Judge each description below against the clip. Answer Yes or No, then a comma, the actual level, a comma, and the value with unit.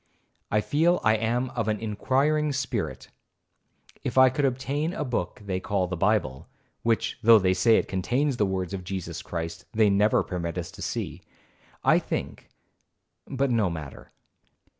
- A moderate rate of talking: Yes, average, 160 wpm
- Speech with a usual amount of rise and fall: No, wide, 5.8 semitones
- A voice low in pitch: Yes, low, 110 Hz